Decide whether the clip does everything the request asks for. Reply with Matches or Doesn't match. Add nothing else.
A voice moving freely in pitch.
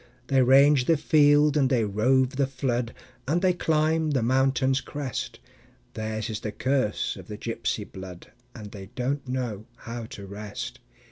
Doesn't match